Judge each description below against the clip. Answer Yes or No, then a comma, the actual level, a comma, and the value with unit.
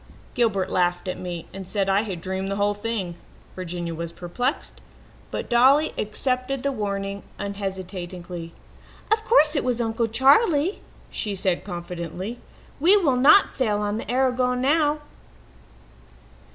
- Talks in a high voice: Yes, high, 205 Hz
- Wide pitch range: Yes, wide, 5.7 semitones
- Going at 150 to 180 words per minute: No, average, 140 wpm